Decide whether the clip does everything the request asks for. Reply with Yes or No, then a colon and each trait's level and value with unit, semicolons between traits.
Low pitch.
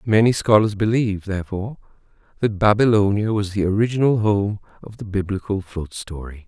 Yes: low, 100 Hz